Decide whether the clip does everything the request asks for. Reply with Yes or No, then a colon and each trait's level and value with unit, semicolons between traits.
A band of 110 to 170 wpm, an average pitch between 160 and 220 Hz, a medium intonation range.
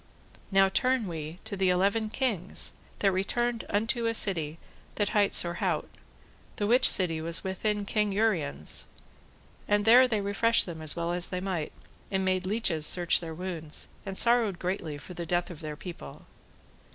Yes: average, 165 wpm; high, 190 Hz; average, 3.8 semitones